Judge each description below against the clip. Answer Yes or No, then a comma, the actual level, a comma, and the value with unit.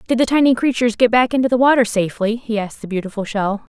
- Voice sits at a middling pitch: No, high, 230 Hz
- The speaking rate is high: Yes, fast, 240 wpm